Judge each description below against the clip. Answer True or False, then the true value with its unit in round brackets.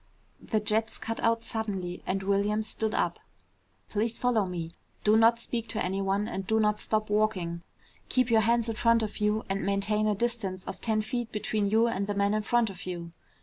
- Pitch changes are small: True (2.3 semitones)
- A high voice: True (215 Hz)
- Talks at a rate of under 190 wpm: False (200 wpm)